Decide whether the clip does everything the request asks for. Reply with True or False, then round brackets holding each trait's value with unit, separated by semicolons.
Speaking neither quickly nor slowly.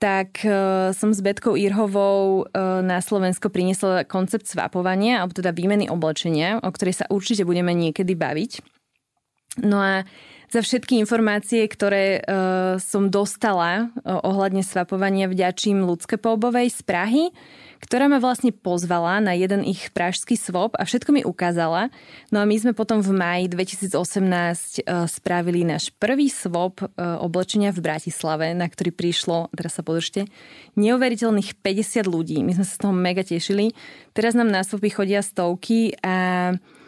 True (150 wpm)